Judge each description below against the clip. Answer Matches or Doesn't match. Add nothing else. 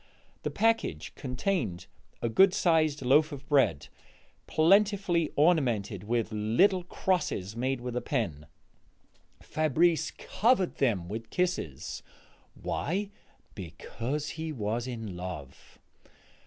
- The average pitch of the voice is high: Doesn't match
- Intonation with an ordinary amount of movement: Doesn't match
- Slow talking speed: Matches